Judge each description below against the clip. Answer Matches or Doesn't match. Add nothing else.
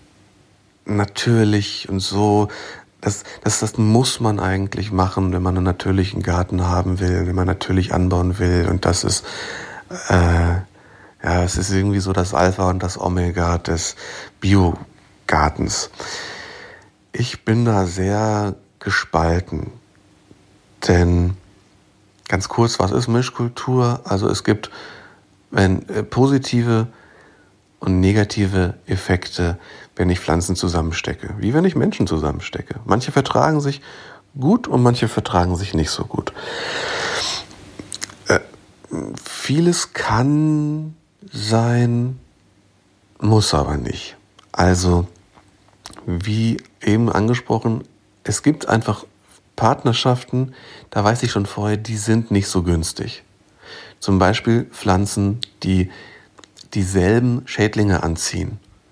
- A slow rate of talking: Matches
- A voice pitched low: Matches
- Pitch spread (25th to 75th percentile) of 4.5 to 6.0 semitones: Doesn't match